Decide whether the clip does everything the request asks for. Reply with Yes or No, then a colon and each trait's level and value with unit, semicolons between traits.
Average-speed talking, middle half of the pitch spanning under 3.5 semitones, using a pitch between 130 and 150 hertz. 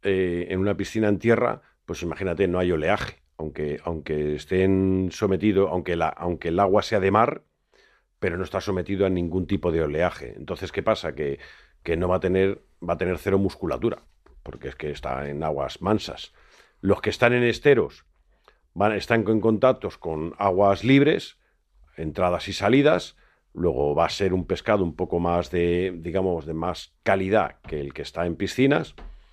No: average, 180 wpm; average, 2.9 semitones; very low, 95 Hz